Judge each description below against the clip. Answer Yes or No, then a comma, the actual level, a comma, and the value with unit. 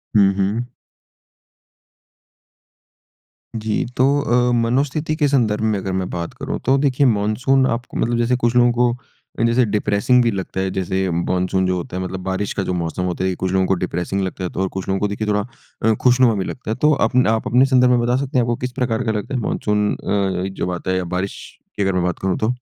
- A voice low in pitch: Yes, low, 105 Hz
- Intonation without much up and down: No, average, 4.5 semitones